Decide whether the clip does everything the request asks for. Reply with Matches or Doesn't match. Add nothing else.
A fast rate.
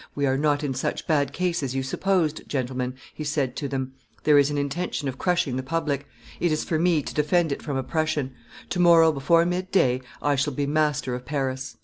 Matches